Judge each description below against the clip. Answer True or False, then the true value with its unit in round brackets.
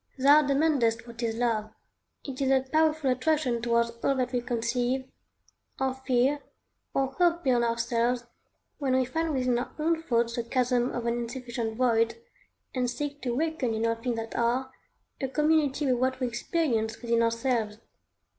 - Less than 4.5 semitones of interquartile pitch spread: True (2.7 semitones)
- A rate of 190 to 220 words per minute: False (165 wpm)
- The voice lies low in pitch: False (250 Hz)